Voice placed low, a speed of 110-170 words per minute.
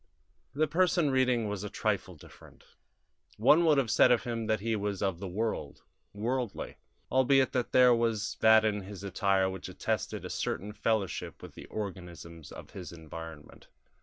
Yes: low, 110 Hz; average, 165 wpm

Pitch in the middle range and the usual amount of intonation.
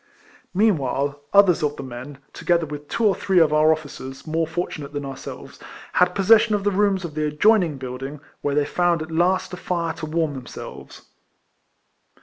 Yes: medium, 160 Hz; average, 3.9 semitones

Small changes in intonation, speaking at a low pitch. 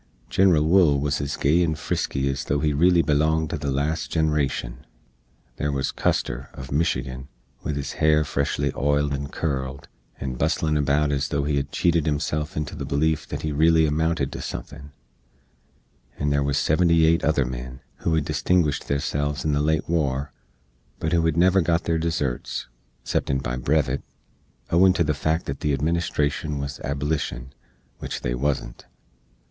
Yes: narrow, 2.3 semitones; very low, 75 Hz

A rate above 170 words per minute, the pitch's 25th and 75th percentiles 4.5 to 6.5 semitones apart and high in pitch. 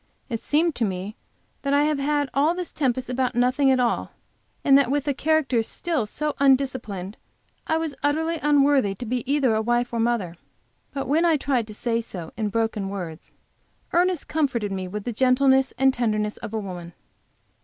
Yes: average, 190 wpm; average, 4.8 semitones; very high, 255 Hz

